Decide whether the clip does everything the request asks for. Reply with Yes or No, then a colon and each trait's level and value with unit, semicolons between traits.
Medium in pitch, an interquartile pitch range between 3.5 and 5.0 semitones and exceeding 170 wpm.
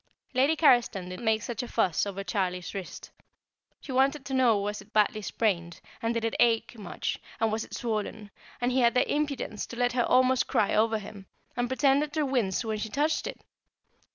No: high, 230 Hz; average, 3.8 semitones; average, 200 wpm